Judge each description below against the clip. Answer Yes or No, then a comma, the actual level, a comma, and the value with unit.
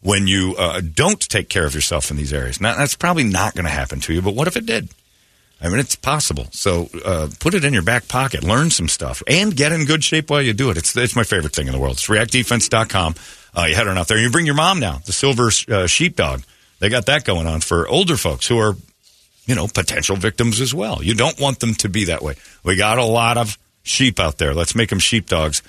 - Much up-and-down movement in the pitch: Yes, wide, 7.0 semitones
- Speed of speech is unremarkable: No, fast, 260 wpm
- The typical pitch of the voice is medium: No, low, 105 Hz